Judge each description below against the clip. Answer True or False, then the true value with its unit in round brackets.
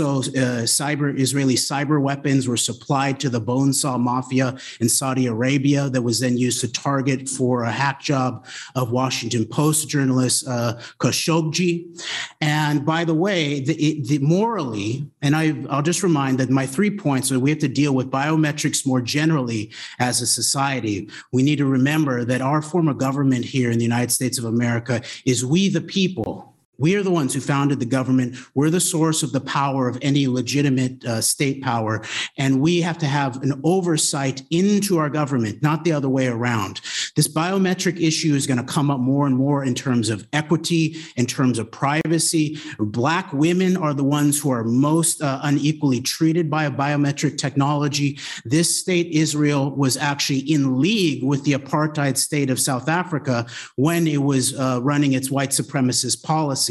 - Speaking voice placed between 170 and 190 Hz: False (140 Hz)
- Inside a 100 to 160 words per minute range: False (180 wpm)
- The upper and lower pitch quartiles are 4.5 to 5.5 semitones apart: False (3.1 semitones)